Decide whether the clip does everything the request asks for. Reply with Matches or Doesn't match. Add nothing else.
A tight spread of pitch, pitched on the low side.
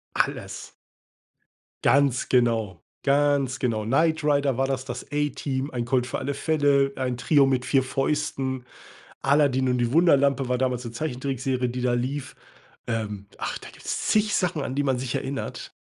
Matches